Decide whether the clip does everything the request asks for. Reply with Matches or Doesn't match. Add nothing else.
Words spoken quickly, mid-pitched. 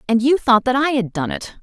Doesn't match